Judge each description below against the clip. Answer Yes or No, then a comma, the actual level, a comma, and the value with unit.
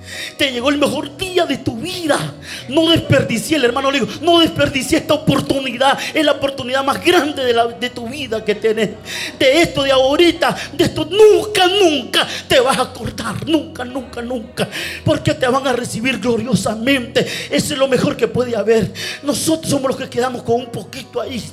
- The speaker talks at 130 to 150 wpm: No, average, 185 wpm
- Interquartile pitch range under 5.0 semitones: Yes, average, 4.1 semitones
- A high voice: Yes, very high, 270 Hz